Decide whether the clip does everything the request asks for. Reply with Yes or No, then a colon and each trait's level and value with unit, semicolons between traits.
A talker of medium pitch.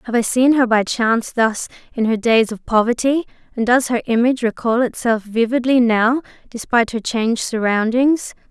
No: high, 235 Hz